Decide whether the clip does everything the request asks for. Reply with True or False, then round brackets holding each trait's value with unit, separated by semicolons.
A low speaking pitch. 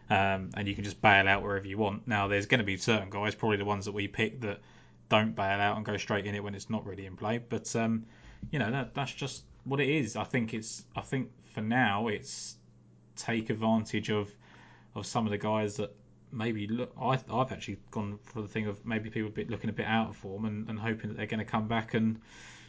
True (110 Hz)